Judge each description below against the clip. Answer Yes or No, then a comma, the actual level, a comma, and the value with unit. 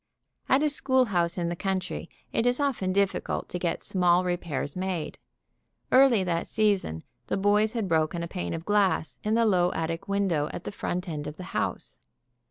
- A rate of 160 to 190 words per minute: Yes, average, 180 wpm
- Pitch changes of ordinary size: Yes, average, 3.6 semitones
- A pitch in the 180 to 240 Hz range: Yes, medium, 185 Hz